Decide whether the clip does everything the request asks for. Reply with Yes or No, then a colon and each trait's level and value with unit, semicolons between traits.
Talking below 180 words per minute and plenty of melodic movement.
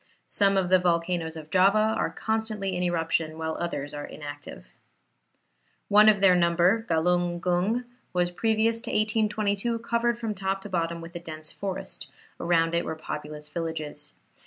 No: average, 160 wpm; average, 4.1 semitones